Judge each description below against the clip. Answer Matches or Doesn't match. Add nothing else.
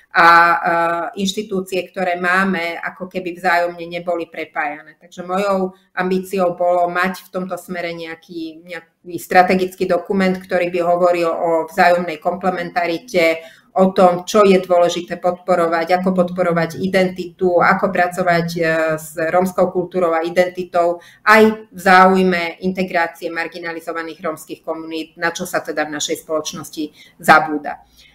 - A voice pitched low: Doesn't match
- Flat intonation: Matches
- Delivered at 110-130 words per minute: Matches